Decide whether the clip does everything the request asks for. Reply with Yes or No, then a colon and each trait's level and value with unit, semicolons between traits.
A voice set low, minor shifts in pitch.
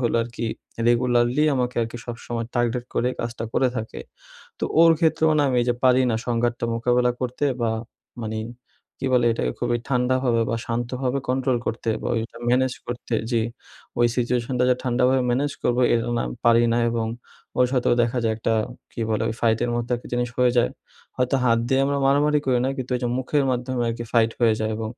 Yes: low, 120 Hz; narrow, 1.5 semitones